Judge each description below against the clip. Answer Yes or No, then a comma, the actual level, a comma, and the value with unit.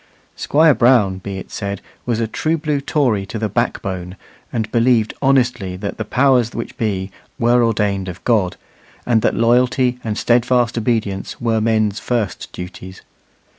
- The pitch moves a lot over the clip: No, average, 3.6 semitones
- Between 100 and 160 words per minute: Yes, average, 155 wpm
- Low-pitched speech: Yes, low, 115 Hz